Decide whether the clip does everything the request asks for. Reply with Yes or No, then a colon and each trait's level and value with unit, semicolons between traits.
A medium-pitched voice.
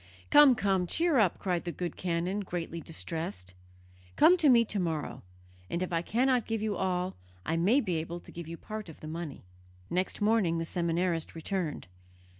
Yes: medium, 180 Hz